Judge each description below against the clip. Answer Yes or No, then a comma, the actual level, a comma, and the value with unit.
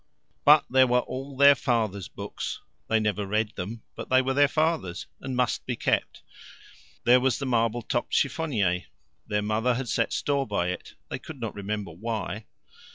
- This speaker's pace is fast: No, average, 175 wpm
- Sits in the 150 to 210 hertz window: No, low, 115 Hz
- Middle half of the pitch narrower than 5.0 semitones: Yes, average, 4.1 semitones